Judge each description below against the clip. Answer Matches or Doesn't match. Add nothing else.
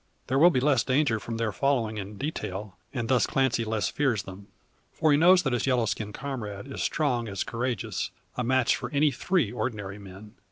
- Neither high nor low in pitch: Doesn't match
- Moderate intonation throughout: Matches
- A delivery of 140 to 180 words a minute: Doesn't match